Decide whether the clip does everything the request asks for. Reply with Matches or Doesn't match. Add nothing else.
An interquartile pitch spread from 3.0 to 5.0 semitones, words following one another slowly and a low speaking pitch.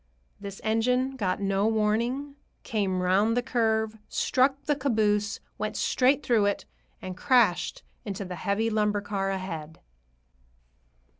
Doesn't match